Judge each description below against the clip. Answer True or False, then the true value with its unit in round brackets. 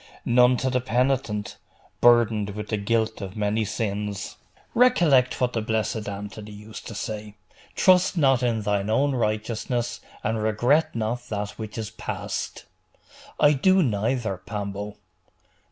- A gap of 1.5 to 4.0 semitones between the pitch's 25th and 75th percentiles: True (3.1 semitones)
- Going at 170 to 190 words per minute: False (135 wpm)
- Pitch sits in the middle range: False (110 Hz)